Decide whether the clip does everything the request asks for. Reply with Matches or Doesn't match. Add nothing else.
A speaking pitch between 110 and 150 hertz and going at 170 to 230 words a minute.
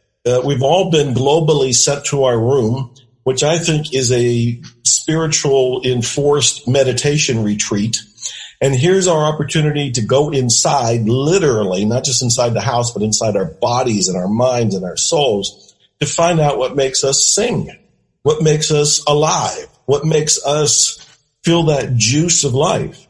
Doesn't match